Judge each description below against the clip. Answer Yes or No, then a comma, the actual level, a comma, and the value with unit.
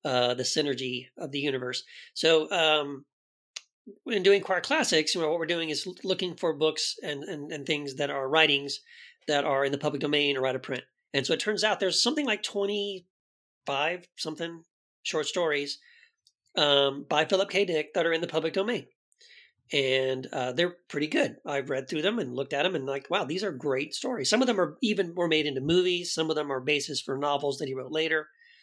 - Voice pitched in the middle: Yes, medium, 155 Hz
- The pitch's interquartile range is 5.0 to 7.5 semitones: No, average, 4.4 semitones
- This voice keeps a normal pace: No, fast, 215 wpm